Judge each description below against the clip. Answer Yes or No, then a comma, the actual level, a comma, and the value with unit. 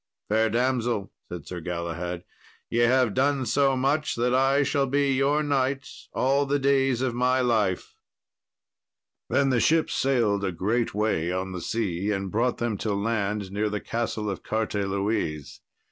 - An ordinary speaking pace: Yes, average, 160 wpm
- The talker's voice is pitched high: No, low, 115 Hz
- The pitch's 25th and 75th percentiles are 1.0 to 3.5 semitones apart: No, average, 5.0 semitones